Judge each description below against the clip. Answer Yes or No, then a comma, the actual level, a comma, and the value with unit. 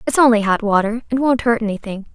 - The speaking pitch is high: Yes, high, 225 Hz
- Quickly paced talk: Yes, fast, 225 wpm